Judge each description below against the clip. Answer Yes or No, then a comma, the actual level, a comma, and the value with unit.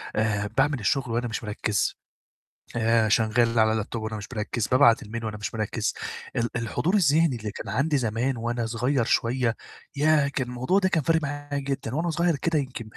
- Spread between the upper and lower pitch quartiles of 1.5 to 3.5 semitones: No, average, 4.3 semitones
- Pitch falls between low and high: No, low, 120 Hz